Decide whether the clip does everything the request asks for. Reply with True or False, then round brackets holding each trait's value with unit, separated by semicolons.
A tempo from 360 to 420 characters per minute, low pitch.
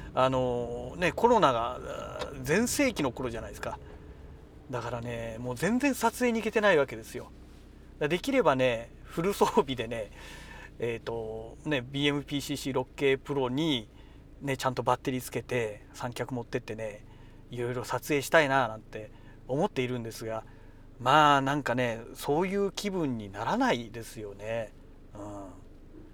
False (300 characters per minute; 125 Hz)